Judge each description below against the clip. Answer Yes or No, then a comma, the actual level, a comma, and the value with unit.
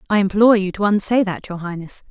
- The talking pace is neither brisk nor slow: No, fast, 230 wpm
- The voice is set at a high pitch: Yes, high, 200 Hz